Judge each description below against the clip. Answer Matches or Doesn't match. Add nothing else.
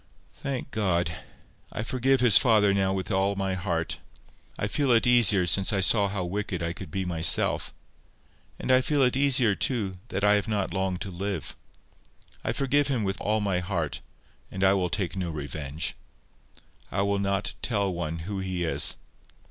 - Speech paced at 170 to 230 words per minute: Matches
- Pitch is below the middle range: Matches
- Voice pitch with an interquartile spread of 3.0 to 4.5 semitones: Matches